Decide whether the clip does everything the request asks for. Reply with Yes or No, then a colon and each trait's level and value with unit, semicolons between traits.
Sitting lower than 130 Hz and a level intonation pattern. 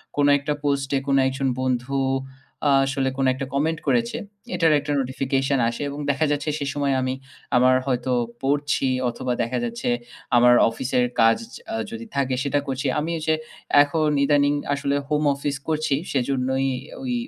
No: medium, 140 Hz; narrow, 2.0 semitones